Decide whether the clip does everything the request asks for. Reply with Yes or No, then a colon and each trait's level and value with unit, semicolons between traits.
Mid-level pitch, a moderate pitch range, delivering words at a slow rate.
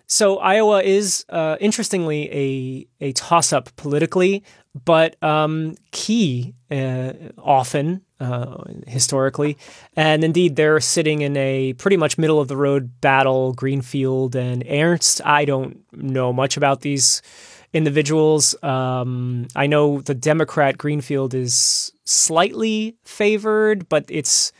Yes: medium, 145 Hz; average, 3.8 semitones; slow, 115 wpm